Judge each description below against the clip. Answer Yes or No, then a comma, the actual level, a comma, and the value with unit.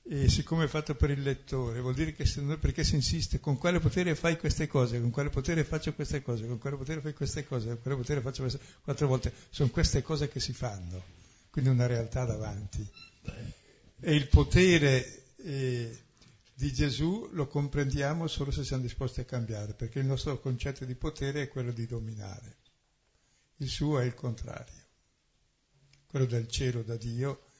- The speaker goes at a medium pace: No, fast, 185 wpm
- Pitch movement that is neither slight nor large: Yes, average, 3.4 semitones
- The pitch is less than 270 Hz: Yes, low, 135 Hz